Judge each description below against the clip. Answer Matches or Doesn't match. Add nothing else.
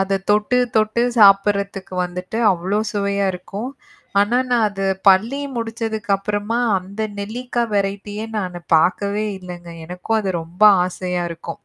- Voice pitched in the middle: Doesn't match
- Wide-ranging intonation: Doesn't match